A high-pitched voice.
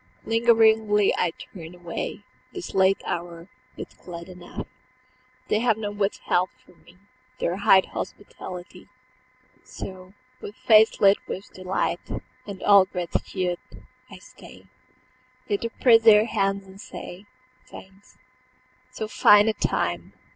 Yes: high, 195 Hz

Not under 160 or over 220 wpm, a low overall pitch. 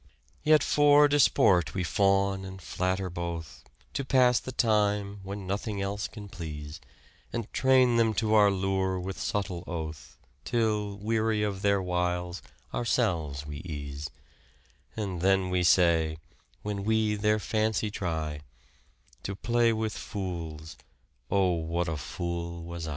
No: average, 140 wpm; very low, 95 Hz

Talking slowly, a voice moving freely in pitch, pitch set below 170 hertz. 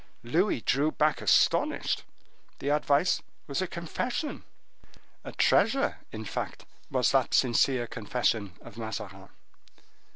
Yes: slow, 105 wpm; wide, 7.3 semitones; low, 135 Hz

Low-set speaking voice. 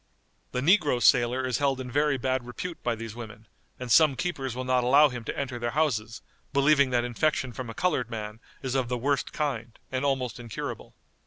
Yes: low, 130 Hz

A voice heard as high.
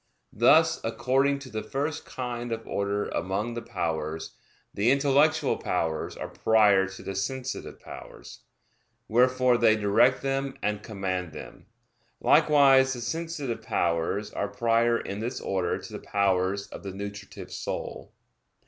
No: low, 115 Hz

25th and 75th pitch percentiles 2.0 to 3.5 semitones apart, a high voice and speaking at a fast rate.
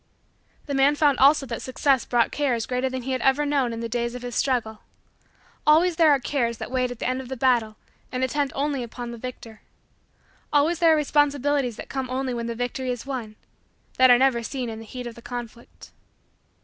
Yes: average, 2.8 semitones; very high, 255 Hz; fast, 215 wpm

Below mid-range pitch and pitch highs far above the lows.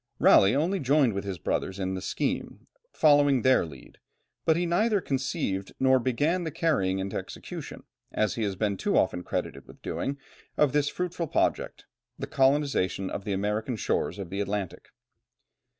Yes: low, 125 Hz; wide, 7.2 semitones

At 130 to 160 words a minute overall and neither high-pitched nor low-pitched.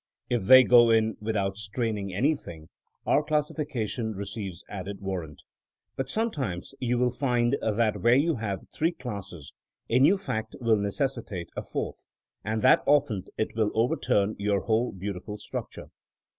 No: average, 150 wpm; low, 110 Hz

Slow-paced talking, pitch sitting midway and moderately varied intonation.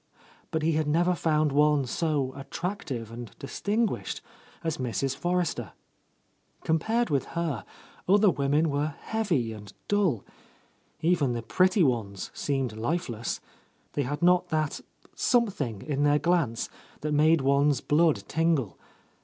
Yes: slow, 130 wpm; medium, 150 Hz; average, 4.5 semitones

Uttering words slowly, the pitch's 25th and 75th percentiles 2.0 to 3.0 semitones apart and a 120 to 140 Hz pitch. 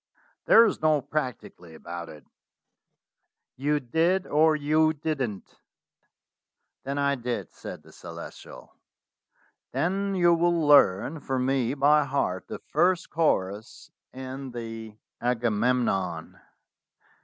No: slow, 110 wpm; wide, 5.5 semitones; low, 135 Hz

